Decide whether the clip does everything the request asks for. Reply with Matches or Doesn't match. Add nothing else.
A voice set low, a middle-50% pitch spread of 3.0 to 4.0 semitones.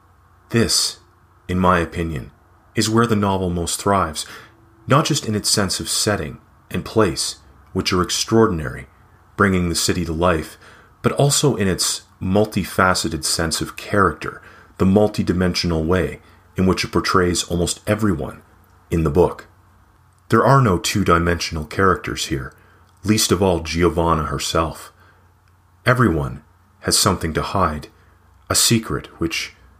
Matches